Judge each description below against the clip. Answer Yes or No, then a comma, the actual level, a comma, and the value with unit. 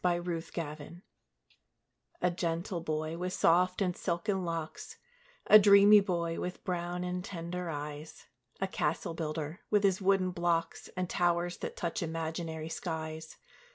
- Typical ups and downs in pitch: No, narrow, 1.9 semitones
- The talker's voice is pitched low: No, medium, 175 Hz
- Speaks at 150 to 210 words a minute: No, average, 140 wpm